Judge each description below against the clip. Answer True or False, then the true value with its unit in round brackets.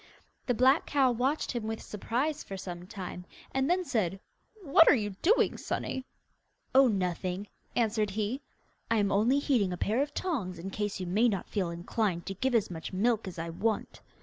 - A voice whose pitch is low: False (215 Hz)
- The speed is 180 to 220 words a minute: True (190 wpm)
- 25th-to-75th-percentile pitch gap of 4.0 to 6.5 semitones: True (5.5 semitones)